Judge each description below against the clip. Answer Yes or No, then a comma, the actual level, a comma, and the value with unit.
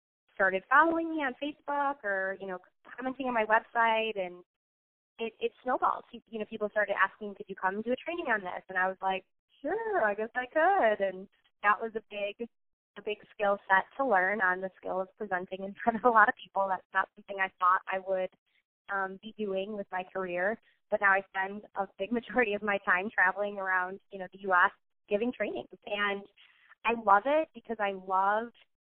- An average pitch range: Yes, average, 3.3 semitones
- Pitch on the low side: No, high, 205 Hz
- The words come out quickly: Yes, fast, 210 wpm